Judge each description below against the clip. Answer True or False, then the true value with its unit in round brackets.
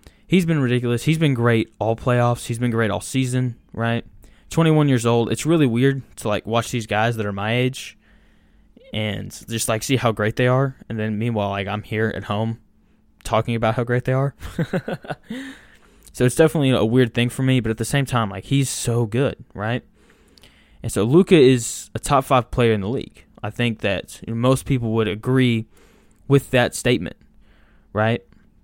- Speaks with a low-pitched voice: True (120 Hz)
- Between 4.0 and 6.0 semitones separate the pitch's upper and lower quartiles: False (3.1 semitones)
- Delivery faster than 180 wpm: True (200 wpm)